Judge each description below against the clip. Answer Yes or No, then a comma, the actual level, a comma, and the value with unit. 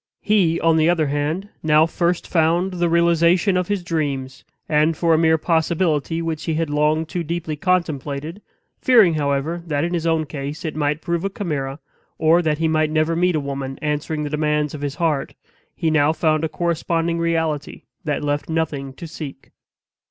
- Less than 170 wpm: No, average, 185 wpm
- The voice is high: No, medium, 160 Hz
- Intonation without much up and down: Yes, narrow, 2.2 semitones